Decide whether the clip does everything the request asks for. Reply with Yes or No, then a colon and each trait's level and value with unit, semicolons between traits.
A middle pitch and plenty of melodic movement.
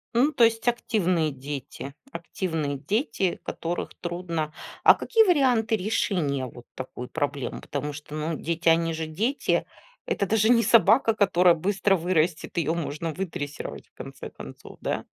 Yes: medium, 170 Hz; wide, 5.9 semitones